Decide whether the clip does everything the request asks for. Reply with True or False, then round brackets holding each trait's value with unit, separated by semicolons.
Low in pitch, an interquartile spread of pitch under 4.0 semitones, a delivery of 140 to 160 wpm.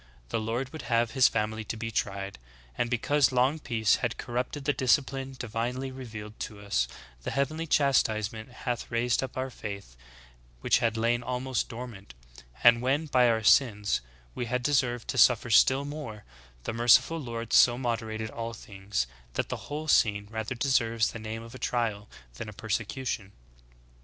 False (120 Hz; 3.0 semitones; 170 wpm)